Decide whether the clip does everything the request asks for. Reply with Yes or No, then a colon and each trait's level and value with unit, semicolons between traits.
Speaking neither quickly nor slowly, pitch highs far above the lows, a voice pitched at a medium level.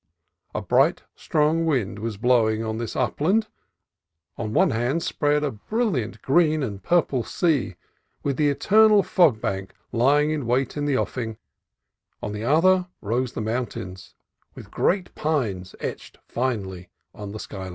No: average, 150 wpm; wide, 6.1 semitones; low, 130 Hz